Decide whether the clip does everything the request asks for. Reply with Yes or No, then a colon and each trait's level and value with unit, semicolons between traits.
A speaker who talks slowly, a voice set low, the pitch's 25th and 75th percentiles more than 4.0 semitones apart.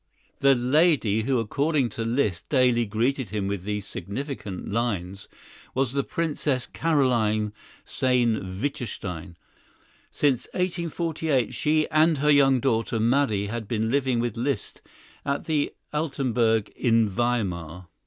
Yes: slow, 125 wpm; low, 120 Hz; average, 4.8 semitones